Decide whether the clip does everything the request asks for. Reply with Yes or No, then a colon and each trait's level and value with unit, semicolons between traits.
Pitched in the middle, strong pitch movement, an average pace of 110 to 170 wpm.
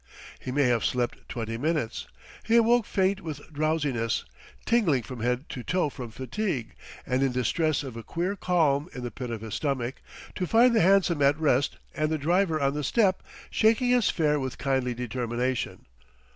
No: medium, 145 Hz; wide, 6.3 semitones; average, 180 wpm